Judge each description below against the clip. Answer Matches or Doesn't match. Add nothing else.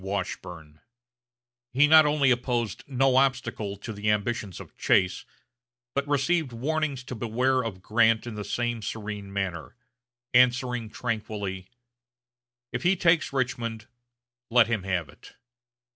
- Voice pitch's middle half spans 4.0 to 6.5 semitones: Matches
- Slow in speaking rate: Matches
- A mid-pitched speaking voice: Doesn't match